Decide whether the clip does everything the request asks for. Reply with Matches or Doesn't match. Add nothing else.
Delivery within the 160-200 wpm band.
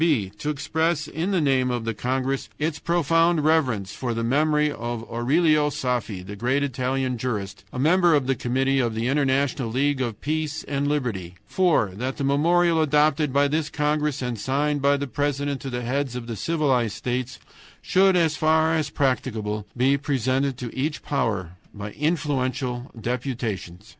Matches